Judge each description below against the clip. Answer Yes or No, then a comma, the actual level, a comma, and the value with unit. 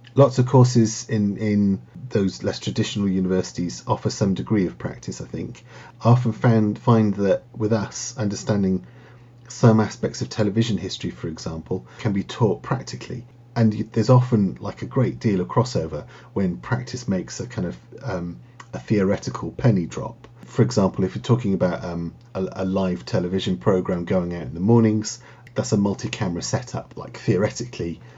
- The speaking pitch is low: Yes, low, 110 Hz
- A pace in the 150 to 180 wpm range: Yes, average, 165 wpm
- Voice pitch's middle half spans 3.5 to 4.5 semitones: Yes, average, 4.0 semitones